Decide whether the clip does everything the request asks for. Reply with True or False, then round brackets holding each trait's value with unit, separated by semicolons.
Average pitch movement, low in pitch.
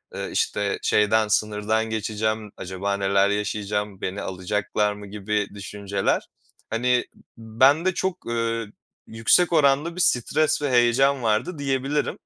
True (4.4 semitones; 110 Hz)